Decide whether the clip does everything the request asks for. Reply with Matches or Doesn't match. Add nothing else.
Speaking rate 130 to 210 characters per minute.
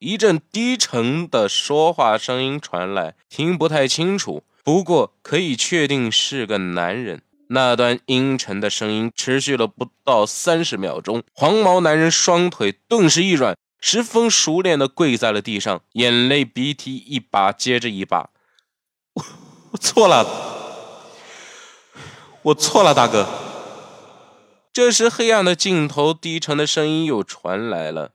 Matches